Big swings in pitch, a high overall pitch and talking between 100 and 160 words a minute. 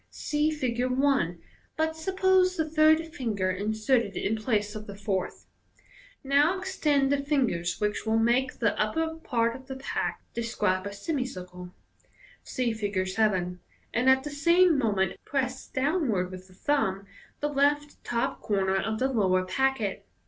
Yes: wide, 6.2 semitones; high, 245 Hz; average, 155 wpm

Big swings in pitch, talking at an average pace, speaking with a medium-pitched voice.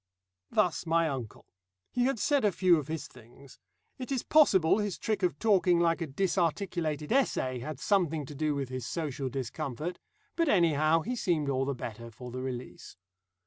Yes: wide, 5.8 semitones; average, 180 wpm; medium, 160 Hz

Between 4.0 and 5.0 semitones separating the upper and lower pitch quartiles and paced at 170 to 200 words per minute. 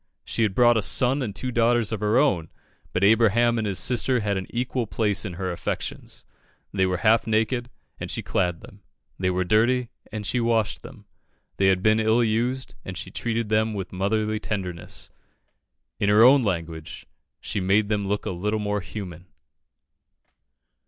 No: average, 3.4 semitones; average, 180 wpm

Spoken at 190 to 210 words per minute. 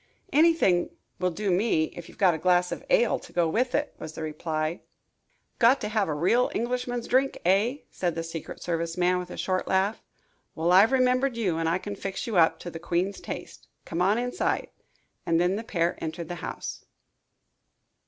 Yes: average, 195 wpm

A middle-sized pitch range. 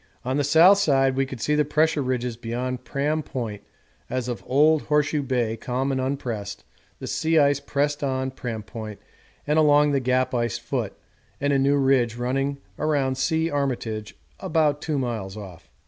Yes: average, 3.1 semitones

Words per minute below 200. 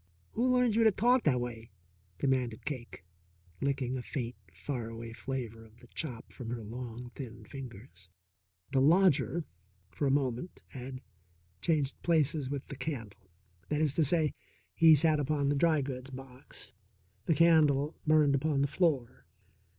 Yes: average, 160 wpm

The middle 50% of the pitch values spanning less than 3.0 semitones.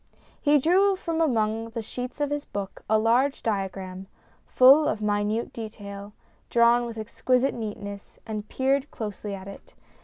No: average, 4.1 semitones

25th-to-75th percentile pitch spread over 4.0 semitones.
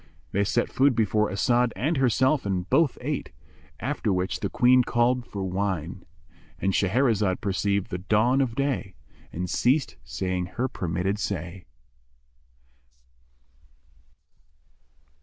Yes: average, 5.1 semitones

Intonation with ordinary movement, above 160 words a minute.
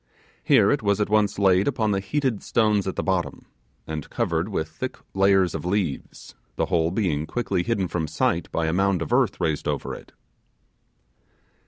Yes: average, 3.8 semitones; average, 180 wpm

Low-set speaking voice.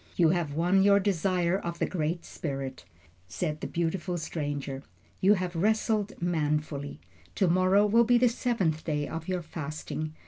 No: medium, 170 Hz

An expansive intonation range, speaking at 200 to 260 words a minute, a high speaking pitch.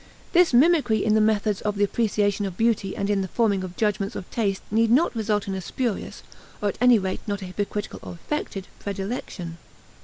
No: narrow, 2.6 semitones; fast, 205 wpm; high, 205 Hz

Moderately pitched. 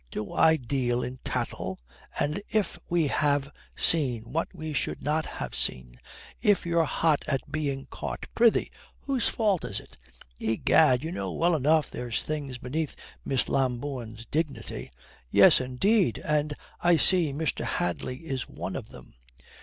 Yes: medium, 145 Hz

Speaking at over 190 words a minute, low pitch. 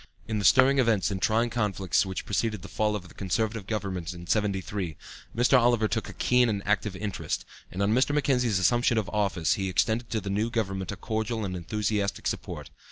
Yes: average, 200 wpm; low, 105 Hz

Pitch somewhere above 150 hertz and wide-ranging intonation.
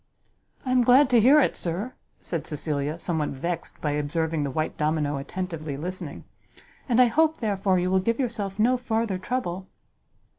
Yes: medium, 185 Hz; wide, 6.9 semitones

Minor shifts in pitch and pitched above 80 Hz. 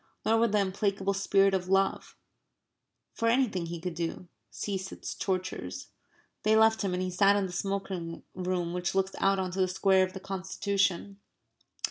Yes: narrow, 1.5 semitones; high, 190 Hz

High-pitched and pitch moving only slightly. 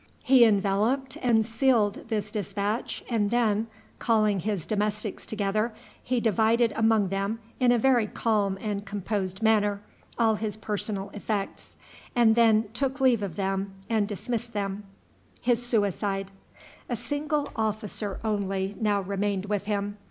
Yes: high, 215 Hz; narrow, 2.3 semitones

